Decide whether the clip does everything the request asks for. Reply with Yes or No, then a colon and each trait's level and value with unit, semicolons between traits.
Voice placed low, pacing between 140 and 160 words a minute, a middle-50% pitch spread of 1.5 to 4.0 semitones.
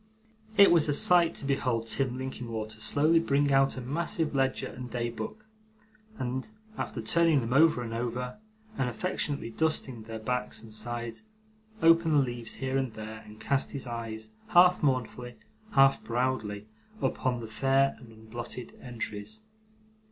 Yes: low, 125 Hz; average, 150 wpm; average, 3.6 semitones